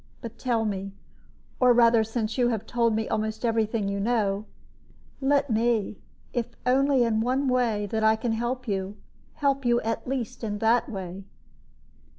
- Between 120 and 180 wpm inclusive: Yes, average, 165 wpm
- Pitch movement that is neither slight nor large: No, narrow, 2.2 semitones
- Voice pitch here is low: No, high, 230 Hz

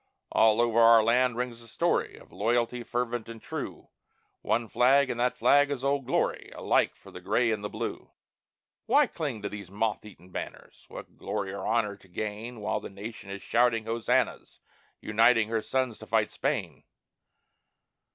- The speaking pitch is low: Yes, low, 115 Hz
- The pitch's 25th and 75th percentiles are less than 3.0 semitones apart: Yes, narrow, 2.4 semitones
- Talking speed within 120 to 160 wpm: No, average, 170 wpm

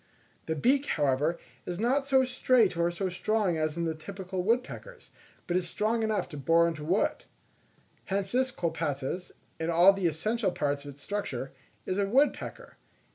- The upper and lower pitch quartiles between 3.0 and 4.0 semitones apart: No, average, 5.3 semitones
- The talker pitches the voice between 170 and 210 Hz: Yes, medium, 185 Hz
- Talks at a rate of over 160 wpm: Yes, average, 175 wpm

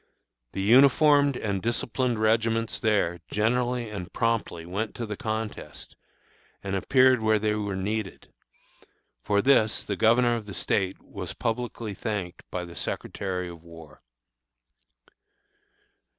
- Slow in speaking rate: Yes, slow, 125 wpm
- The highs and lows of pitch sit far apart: No, average, 3.4 semitones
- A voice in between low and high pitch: No, low, 110 Hz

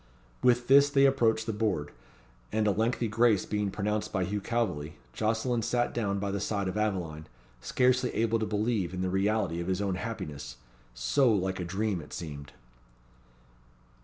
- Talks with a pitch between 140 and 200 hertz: No, low, 105 Hz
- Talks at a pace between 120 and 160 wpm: No, average, 170 wpm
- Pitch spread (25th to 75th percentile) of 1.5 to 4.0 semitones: Yes, average, 3.7 semitones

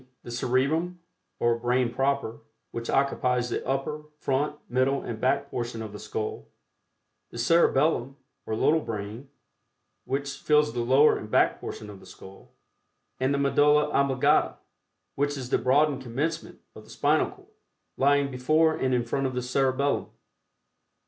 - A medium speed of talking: Yes, average, 150 wpm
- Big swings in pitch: No, average, 3.0 semitones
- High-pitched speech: No, low, 130 Hz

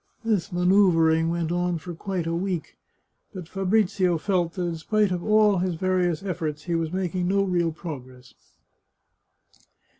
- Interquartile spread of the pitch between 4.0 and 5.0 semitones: No, narrow, 2.4 semitones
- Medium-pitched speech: Yes, medium, 175 Hz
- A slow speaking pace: No, average, 150 wpm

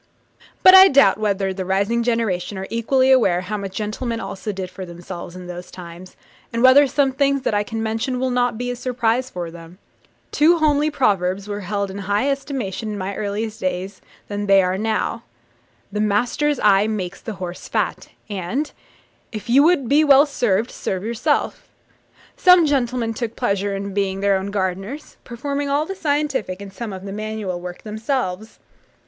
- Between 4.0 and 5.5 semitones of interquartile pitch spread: Yes, average, 5.1 semitones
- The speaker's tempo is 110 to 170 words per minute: No, average, 180 wpm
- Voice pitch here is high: Yes, high, 215 Hz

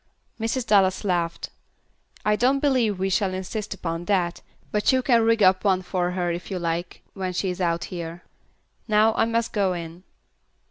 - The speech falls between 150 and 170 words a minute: No, average, 180 wpm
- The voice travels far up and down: No, average, 3.7 semitones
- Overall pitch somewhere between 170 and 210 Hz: Yes, high, 190 Hz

